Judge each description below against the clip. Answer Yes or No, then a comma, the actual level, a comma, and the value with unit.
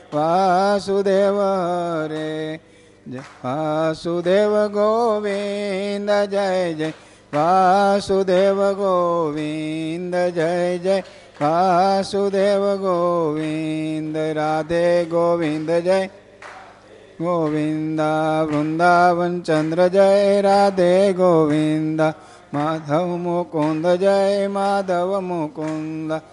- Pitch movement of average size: Yes, average, 3.8 semitones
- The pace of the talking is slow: Yes, slow, 55 wpm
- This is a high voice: No, medium, 175 Hz